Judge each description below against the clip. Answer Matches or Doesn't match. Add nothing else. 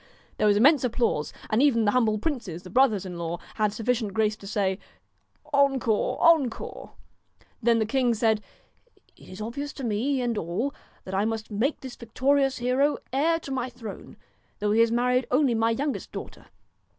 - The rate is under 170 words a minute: Doesn't match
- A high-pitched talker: Matches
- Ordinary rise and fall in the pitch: Matches